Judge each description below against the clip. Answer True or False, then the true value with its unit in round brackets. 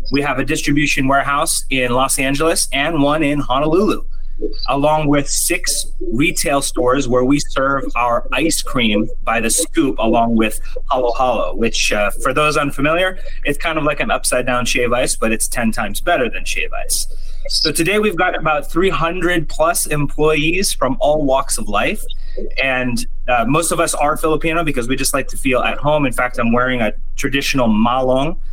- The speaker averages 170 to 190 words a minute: True (185 wpm)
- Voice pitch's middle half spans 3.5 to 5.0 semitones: True (4.0 semitones)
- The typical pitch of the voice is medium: True (145 Hz)